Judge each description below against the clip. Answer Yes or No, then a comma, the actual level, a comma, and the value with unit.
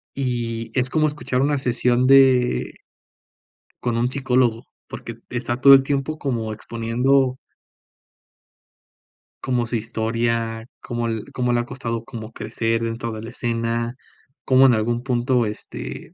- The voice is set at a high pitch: No, low, 120 Hz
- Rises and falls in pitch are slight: Yes, narrow, 2.0 semitones